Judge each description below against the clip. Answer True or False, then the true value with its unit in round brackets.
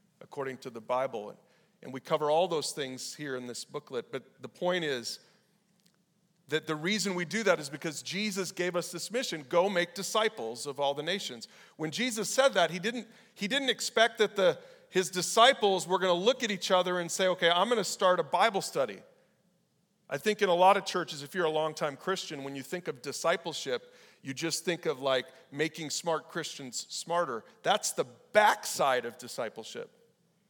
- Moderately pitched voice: True (180 Hz)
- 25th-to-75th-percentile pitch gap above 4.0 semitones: True (4.6 semitones)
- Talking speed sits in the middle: True (190 wpm)